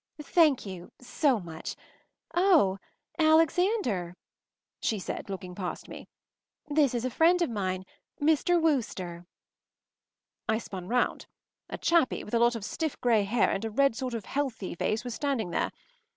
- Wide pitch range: Yes, wide, 7.5 semitones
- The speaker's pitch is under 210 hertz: No, high, 235 Hz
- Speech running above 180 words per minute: No, average, 150 wpm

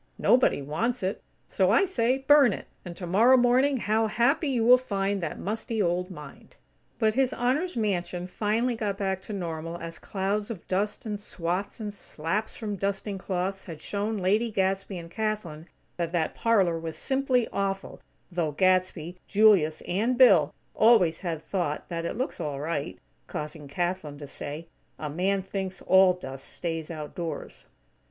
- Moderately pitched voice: No, high, 195 Hz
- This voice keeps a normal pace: Yes, average, 160 wpm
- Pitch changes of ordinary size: Yes, average, 4.5 semitones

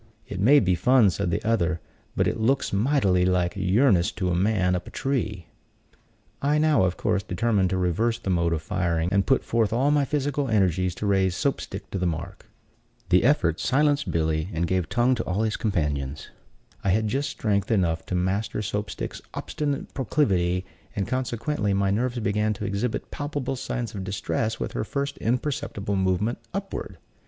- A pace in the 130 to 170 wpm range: No, average, 185 wpm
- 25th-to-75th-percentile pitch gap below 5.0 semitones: No, average, 5.3 semitones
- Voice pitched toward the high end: No, low, 100 Hz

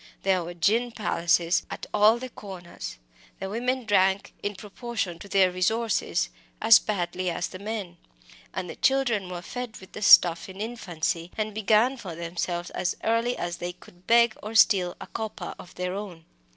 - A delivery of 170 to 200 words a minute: Yes, average, 175 wpm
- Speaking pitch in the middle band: No, high, 195 Hz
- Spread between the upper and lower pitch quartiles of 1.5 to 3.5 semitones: No, average, 3.9 semitones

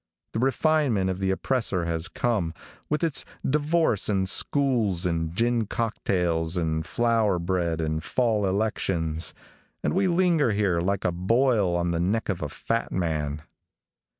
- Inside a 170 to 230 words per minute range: No, average, 150 wpm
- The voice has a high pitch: No, very low, 95 Hz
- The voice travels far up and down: Yes, wide, 5.8 semitones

